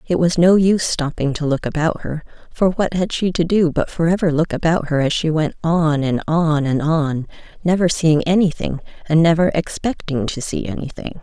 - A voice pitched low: No, medium, 160 Hz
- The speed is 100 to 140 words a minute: No, fast, 205 wpm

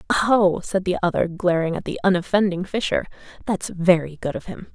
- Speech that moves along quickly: No, average, 175 wpm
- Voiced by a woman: Yes, female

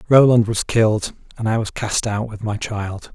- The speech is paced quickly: Yes, fast, 210 wpm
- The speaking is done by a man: Yes, male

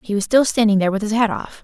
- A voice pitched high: Yes, high, 215 Hz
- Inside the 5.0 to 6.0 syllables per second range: No, 7.2 syllables/s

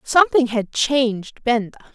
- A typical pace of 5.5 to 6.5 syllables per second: No, 4.7 syllables/s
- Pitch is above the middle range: Yes, high, 240 Hz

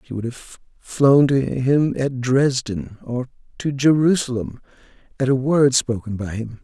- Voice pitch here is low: Yes, low, 130 Hz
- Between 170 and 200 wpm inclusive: No, average, 155 wpm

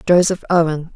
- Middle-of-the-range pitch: Yes, medium, 170 Hz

